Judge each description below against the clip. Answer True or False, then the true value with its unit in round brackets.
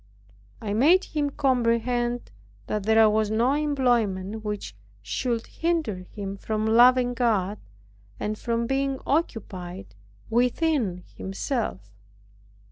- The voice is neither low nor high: False (230 Hz)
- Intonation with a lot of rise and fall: False (3.8 semitones)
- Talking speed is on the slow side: True (105 wpm)